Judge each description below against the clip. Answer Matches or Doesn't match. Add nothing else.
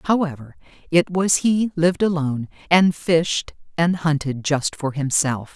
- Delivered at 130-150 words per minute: Matches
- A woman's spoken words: Matches